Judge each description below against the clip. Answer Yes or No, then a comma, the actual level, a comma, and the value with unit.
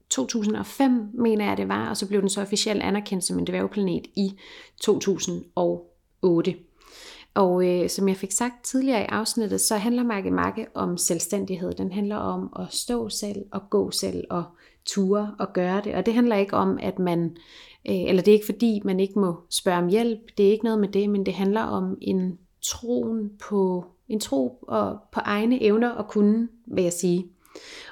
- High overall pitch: Yes, high, 200 Hz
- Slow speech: No, average, 190 wpm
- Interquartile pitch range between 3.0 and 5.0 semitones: Yes, average, 3.3 semitones